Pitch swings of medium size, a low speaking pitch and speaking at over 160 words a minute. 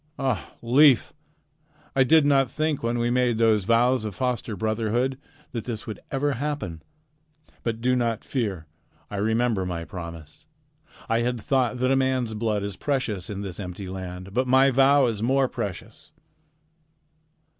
No: average, 4.2 semitones; low, 115 Hz; average, 155 wpm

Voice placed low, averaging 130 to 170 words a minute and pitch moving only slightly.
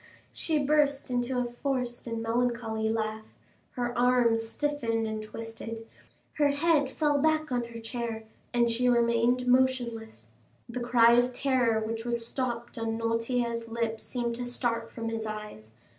No: high, 235 Hz; average, 150 wpm; narrow, 1.8 semitones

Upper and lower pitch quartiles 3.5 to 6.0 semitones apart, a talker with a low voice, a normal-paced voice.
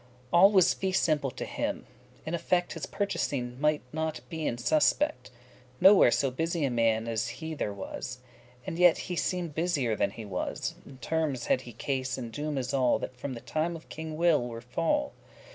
No: average, 5.1 semitones; medium, 145 Hz; average, 195 wpm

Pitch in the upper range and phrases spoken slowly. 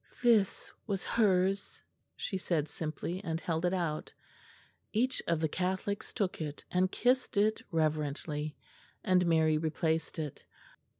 No: medium, 175 Hz; slow, 130 wpm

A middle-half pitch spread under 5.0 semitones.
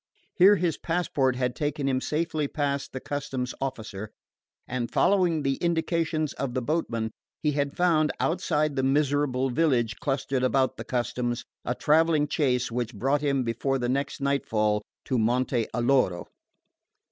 Yes: average, 3.4 semitones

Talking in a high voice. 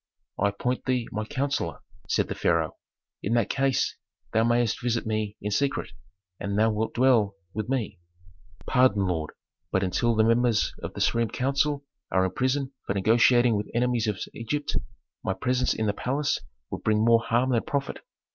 No: low, 115 Hz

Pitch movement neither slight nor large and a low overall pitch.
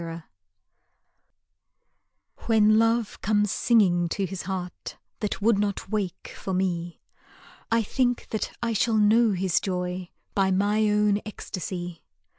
No: average, 3.1 semitones; high, 200 Hz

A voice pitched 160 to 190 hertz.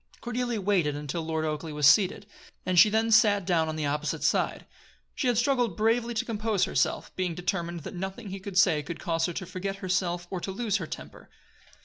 Yes: medium, 185 Hz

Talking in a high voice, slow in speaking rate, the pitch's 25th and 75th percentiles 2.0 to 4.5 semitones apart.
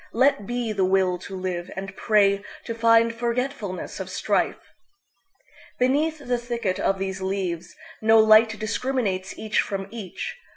Yes: high, 215 Hz; slow, 125 wpm; average, 4.0 semitones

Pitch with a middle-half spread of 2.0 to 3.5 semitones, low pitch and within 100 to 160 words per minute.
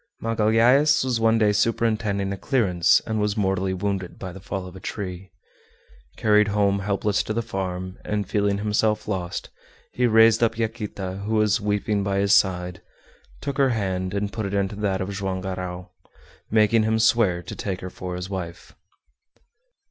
No: narrow, 2.6 semitones; low, 100 Hz; average, 170 wpm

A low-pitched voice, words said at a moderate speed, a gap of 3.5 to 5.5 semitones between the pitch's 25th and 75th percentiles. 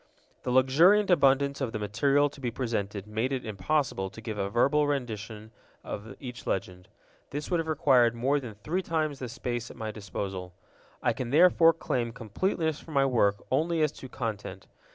Yes: low, 125 Hz; average, 180 wpm; average, 5.2 semitones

